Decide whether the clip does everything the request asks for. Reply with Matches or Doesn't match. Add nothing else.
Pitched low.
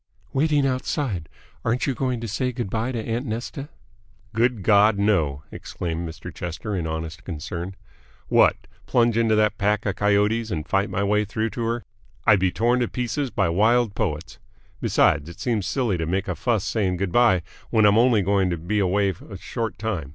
Matches